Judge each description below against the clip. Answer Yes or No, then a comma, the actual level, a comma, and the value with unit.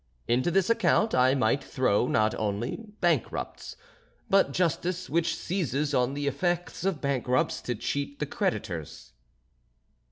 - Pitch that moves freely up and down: Yes, wide, 5.9 semitones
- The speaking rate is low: Yes, slow, 130 wpm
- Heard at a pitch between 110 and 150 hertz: Yes, medium, 140 Hz